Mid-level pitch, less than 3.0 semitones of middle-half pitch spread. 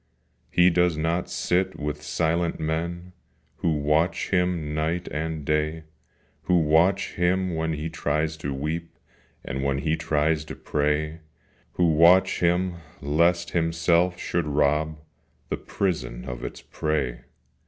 No: very low, 80 Hz; narrow, 2.4 semitones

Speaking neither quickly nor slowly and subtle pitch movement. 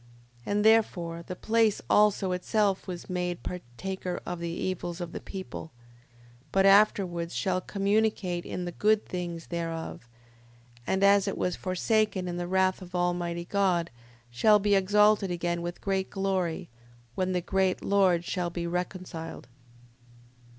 Yes: average, 145 wpm; narrow, 2.3 semitones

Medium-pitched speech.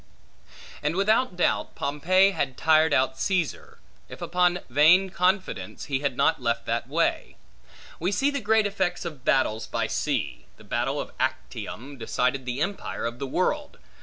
Yes: medium, 160 Hz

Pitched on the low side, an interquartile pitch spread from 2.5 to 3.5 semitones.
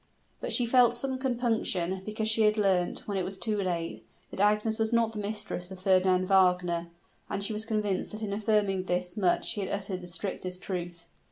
No: high, 200 Hz; average, 3.0 semitones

